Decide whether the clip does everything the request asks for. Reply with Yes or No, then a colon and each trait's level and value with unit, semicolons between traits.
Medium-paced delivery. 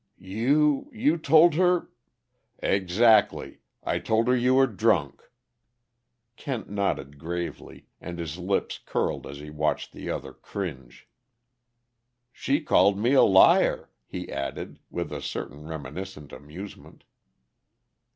No: slow, 125 wpm